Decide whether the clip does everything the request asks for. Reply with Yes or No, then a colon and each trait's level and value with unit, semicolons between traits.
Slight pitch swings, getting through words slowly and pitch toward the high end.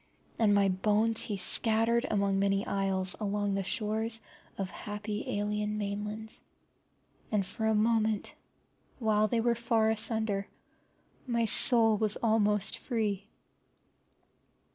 Yes: narrow, 1.7 semitones; slow, 120 wpm; high, 210 Hz